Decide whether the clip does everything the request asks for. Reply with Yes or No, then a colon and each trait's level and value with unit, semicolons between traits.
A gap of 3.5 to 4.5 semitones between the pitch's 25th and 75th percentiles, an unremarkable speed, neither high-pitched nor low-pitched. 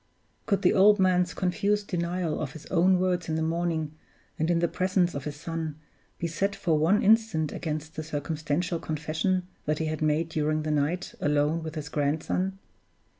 No: average, 2.9 semitones; average, 180 wpm; medium, 165 Hz